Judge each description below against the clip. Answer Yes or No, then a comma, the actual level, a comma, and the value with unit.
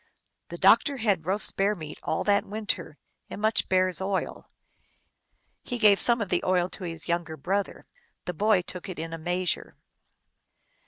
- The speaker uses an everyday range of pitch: Yes, average, 3.1 semitones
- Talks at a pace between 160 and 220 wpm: Yes, average, 175 wpm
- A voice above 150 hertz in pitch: Yes, medium, 185 Hz